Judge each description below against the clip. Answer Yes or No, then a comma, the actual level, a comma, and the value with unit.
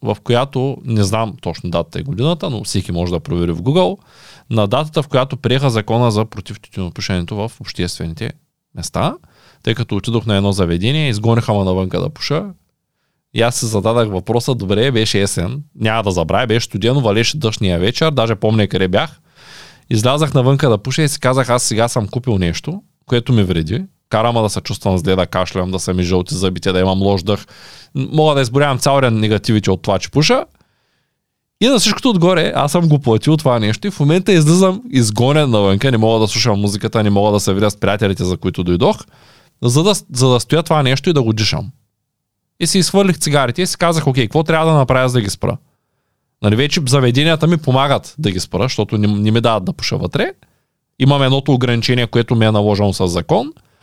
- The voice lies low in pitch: Yes, low, 120 Hz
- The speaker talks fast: Yes, fast, 200 wpm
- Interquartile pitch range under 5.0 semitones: No, wide, 5.6 semitones